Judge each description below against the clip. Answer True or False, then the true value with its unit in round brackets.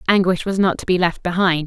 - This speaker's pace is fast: True (255 wpm)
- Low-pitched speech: False (180 Hz)